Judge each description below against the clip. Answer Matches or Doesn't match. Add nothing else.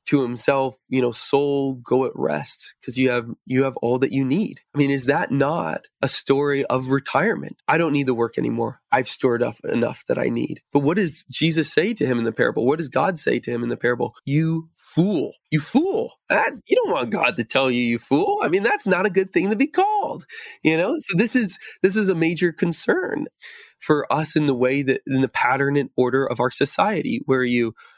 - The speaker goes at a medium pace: Doesn't match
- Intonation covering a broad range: Matches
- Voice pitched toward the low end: Doesn't match